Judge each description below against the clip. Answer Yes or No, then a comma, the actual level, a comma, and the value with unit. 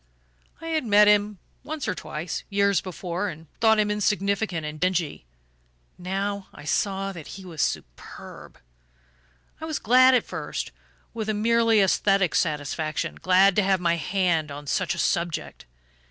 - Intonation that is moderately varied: Yes, average, 3.7 semitones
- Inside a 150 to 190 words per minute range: Yes, average, 155 wpm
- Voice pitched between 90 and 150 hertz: No, high, 195 Hz